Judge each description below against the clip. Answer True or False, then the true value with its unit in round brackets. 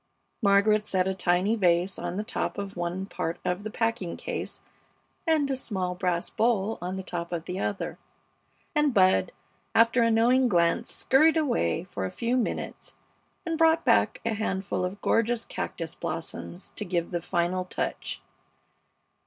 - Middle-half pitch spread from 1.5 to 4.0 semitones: False (4.5 semitones)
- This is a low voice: False (195 Hz)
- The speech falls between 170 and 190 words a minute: False (160 wpm)